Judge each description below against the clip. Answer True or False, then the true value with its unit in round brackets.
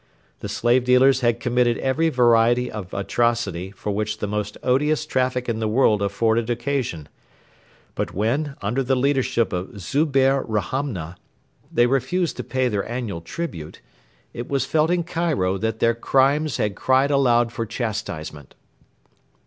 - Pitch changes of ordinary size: True (4.1 semitones)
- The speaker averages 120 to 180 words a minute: True (150 wpm)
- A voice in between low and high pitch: False (120 Hz)